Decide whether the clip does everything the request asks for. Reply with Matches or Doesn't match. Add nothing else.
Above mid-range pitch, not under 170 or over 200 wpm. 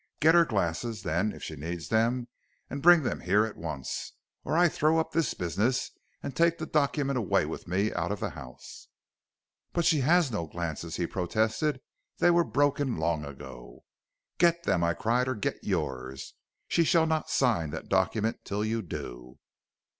Doesn't match